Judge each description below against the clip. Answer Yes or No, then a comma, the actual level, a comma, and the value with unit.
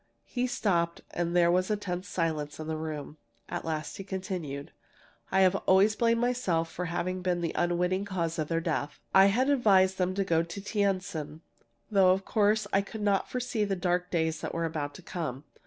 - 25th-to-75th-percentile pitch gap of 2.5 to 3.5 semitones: Yes, average, 3.2 semitones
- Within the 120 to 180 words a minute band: No, average, 200 wpm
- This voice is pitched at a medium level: Yes, medium, 180 Hz